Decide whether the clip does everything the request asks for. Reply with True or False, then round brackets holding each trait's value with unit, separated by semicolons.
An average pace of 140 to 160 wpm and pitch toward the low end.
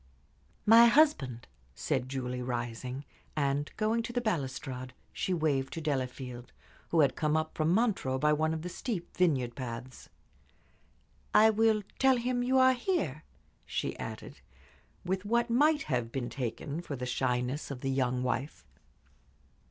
False (150 wpm; 150 Hz)